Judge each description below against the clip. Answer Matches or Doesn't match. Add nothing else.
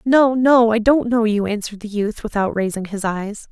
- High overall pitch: Matches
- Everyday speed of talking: Doesn't match